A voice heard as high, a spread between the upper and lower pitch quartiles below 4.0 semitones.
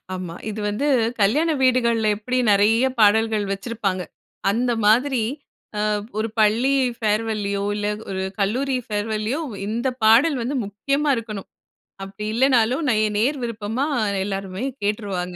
Yes: high, 220 Hz; average, 3.5 semitones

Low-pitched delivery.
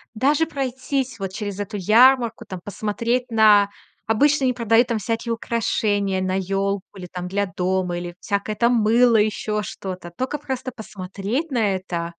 No: high, 215 Hz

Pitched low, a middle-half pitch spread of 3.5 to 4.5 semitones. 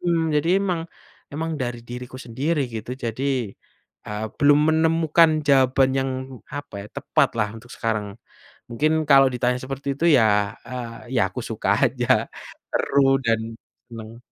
Yes: low, 130 Hz; average, 4.2 semitones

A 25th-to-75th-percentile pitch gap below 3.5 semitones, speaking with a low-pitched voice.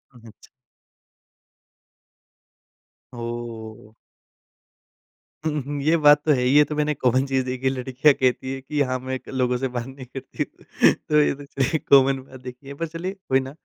Yes: narrow, 2.6 semitones; low, 130 Hz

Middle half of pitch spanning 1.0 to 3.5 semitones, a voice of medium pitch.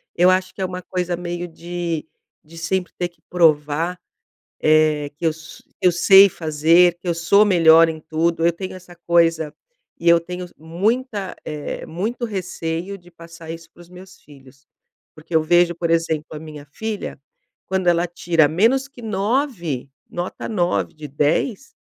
Yes: narrow, 2.4 semitones; medium, 170 Hz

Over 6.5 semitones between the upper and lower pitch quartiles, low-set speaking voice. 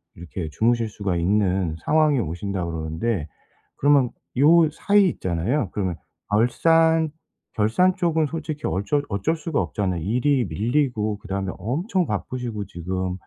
Yes: wide, 8.1 semitones; low, 110 Hz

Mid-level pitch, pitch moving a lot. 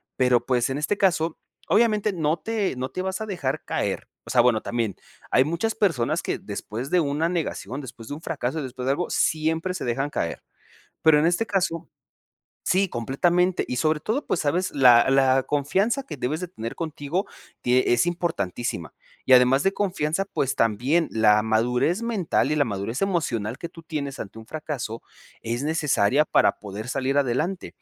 Yes: medium, 145 Hz; wide, 5.9 semitones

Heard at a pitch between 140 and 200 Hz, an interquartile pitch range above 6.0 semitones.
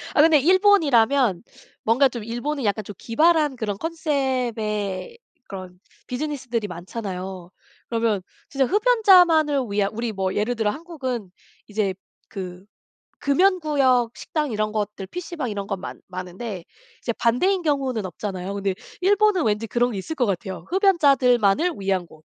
No: high, 235 Hz; wide, 7.1 semitones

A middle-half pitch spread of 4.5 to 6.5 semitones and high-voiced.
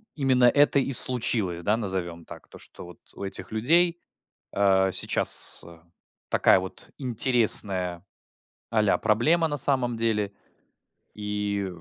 No: average, 4.8 semitones; low, 110 Hz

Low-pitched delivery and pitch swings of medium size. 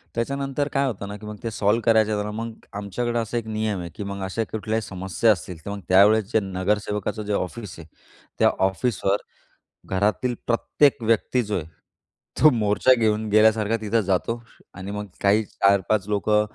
No: low, 105 Hz; narrow, 2.3 semitones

